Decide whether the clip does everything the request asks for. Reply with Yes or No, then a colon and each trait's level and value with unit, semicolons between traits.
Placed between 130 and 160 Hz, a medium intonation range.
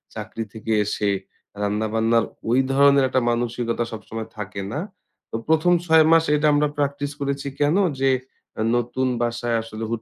No: low, 120 Hz; average, 4.0 semitones